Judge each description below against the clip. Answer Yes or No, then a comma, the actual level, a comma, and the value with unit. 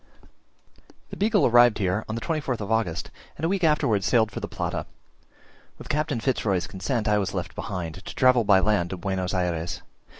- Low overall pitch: Yes, low, 105 Hz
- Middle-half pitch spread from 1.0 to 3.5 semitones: No, average, 5.3 semitones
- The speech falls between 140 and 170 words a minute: No, average, 195 wpm